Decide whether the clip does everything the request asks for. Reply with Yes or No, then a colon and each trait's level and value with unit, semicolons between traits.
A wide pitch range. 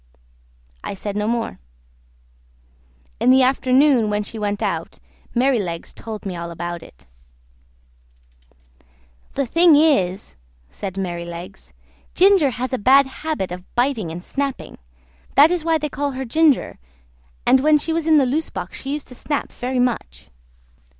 Yes: wide, 6.8 semitones